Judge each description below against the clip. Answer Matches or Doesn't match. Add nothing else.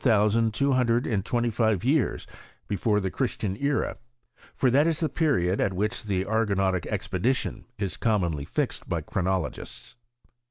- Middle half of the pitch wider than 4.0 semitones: Matches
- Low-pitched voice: Matches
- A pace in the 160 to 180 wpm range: Matches